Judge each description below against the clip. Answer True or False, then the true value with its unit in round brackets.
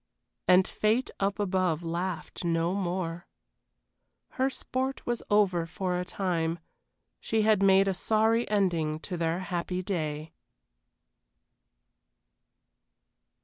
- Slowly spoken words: True (105 wpm)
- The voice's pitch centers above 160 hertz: True (185 Hz)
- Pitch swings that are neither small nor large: True (3.3 semitones)